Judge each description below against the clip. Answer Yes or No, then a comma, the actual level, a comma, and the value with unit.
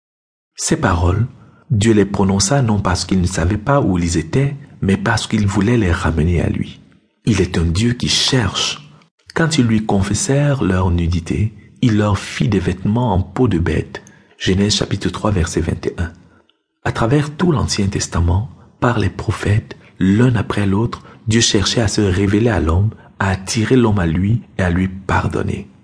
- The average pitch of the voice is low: Yes, low, 105 Hz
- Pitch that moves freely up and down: No, average, 3.9 semitones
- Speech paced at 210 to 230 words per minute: No, average, 175 wpm